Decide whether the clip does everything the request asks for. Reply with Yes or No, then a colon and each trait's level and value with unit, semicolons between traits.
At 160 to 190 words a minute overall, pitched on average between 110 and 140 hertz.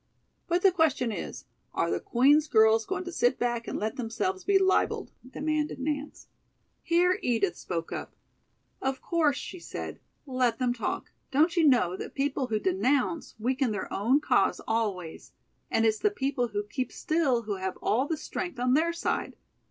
No: average, 175 wpm; very high, 260 Hz